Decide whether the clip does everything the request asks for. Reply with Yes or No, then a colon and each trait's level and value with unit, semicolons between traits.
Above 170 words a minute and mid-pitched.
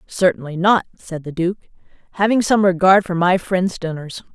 No: average, 165 wpm; medium, 180 Hz